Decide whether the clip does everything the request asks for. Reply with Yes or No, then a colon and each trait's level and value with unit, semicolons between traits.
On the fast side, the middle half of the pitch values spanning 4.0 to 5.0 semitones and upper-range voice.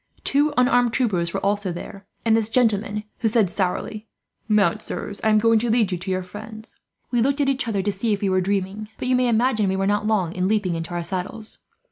No: fast, 235 wpm; average, 3.0 semitones; high, 210 Hz